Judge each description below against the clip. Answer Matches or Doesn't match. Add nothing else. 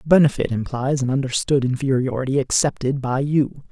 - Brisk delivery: Doesn't match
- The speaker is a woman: Doesn't match